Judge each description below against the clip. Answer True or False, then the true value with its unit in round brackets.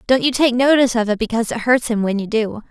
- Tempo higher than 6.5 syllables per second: True (6.8 syllables/s)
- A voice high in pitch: True (235 Hz)